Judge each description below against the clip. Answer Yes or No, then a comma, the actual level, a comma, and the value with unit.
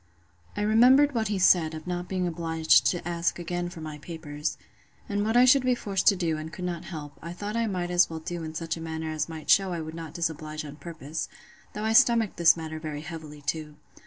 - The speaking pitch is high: No, medium, 170 Hz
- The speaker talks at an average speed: No, fast, 235 wpm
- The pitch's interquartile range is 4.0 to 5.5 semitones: No, average, 3.5 semitones